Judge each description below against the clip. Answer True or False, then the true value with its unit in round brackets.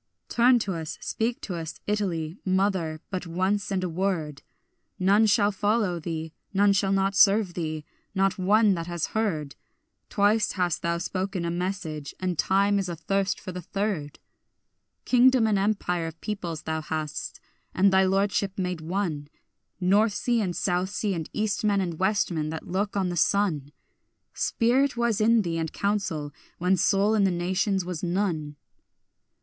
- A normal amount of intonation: True (3.3 semitones)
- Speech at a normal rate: True (165 wpm)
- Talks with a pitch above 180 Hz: True (190 Hz)